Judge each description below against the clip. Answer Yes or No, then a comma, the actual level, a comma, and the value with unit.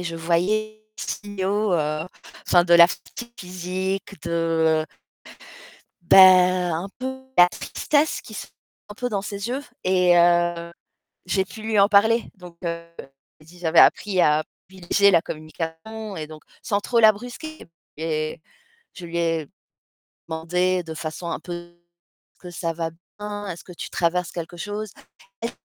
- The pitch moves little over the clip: No, average, 3.5 semitones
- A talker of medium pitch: Yes, medium, 180 Hz